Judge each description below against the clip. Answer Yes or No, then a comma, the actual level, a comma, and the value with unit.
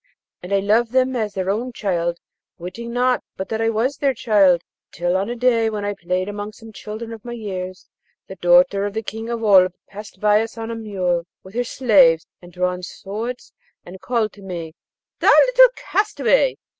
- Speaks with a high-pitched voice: Yes, high, 210 Hz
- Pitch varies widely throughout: No, average, 3.9 semitones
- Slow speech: No, average, 195 wpm